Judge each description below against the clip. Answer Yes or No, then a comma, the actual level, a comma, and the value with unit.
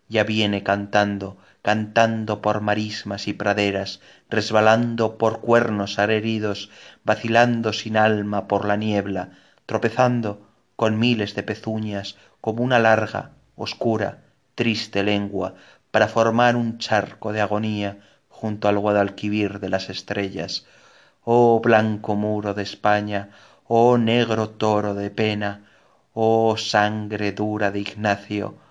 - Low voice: Yes, low, 105 Hz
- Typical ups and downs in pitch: No, narrow, 1.7 semitones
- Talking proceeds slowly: Yes, slow, 115 wpm